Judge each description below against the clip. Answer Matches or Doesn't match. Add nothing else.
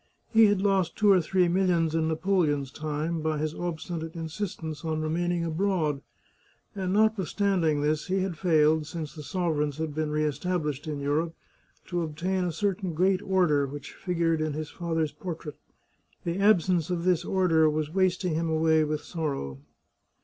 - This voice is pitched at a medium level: Matches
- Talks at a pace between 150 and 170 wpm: Matches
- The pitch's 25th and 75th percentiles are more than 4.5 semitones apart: Doesn't match